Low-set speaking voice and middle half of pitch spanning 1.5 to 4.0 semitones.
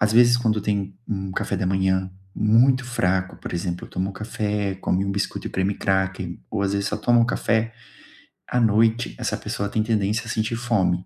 Yes: low, 100 Hz; average, 2.9 semitones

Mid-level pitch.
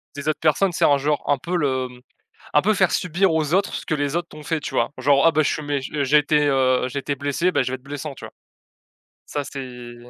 Yes: medium, 145 Hz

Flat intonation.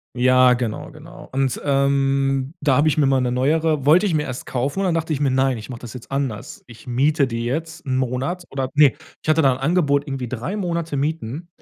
No: average, 3.3 semitones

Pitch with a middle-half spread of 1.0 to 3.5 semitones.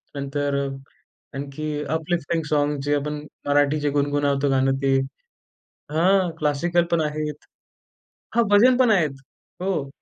Yes: average, 2.9 semitones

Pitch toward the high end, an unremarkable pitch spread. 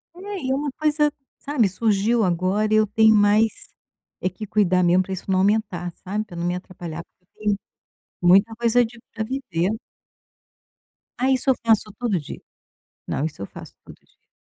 Yes: high, 210 Hz; average, 4.1 semitones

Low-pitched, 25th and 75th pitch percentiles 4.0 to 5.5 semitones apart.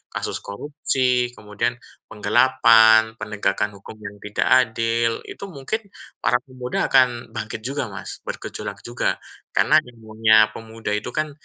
No: low, 115 Hz; average, 2.8 semitones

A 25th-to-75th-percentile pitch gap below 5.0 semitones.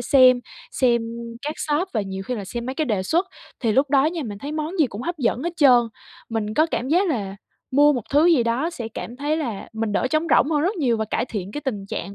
No: wide, 5.5 semitones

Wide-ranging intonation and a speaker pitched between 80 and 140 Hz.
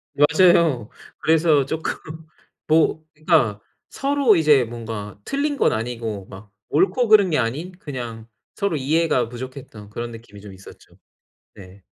Yes: wide, 6.4 semitones; low, 135 Hz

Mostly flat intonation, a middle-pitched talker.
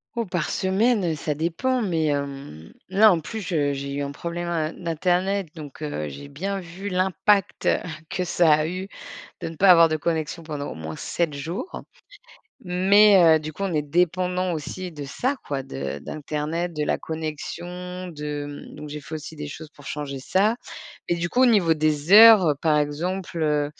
No: average, 3.7 semitones; medium, 165 Hz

